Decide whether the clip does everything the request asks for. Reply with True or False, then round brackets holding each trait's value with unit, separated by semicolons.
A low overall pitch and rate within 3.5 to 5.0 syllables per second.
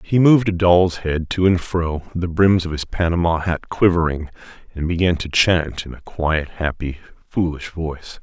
True (85 Hz; 4.8 syllables/s)